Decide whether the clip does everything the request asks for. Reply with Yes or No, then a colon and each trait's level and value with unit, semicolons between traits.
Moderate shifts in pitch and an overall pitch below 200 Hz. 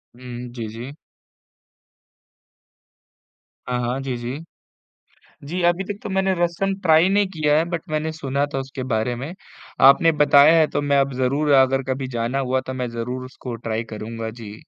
Yes: average, 4.3 semitones; low, 135 Hz